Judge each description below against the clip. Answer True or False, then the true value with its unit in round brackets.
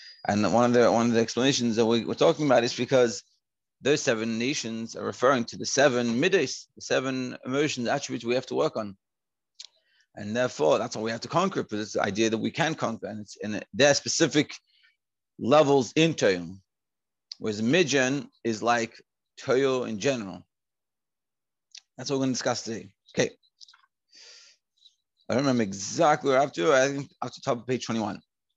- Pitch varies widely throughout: False (3.3 semitones)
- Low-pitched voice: True (120 Hz)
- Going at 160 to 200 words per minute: True (195 wpm)